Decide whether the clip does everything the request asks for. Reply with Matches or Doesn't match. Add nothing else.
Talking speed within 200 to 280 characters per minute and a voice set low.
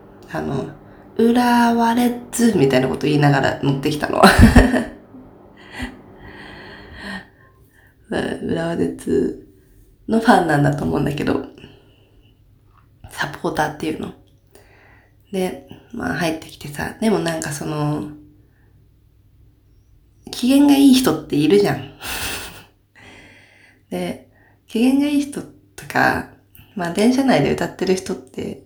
Matches